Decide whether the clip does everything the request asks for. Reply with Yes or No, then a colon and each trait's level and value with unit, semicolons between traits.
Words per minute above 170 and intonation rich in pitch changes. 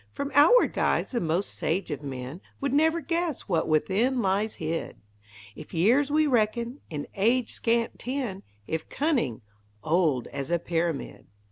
No: average, 150 wpm; wide, 8.8 semitones